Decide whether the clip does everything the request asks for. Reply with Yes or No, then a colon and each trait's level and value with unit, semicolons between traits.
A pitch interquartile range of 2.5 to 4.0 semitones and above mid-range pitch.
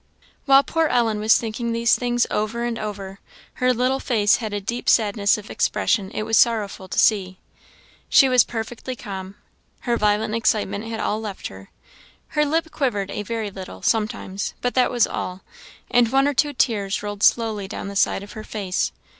Yes: average, 3.0 semitones; high, 220 Hz